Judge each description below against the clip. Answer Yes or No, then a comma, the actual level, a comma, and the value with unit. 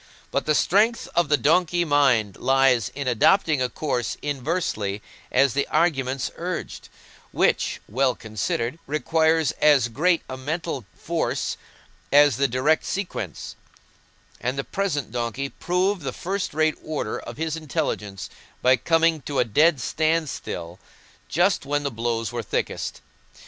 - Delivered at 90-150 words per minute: Yes, average, 140 wpm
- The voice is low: No, medium, 145 Hz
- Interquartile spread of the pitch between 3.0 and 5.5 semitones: Yes, average, 4.6 semitones